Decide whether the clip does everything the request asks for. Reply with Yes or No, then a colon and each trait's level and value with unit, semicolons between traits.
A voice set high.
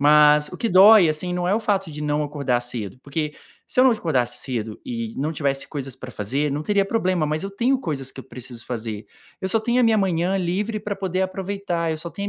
No: medium, 160 Hz